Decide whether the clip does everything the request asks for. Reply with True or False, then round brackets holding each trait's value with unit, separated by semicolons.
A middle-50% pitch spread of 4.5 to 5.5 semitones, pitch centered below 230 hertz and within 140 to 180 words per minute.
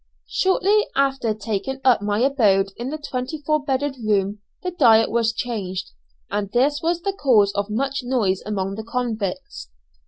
False (5.1 semitones; 235 Hz; 160 wpm)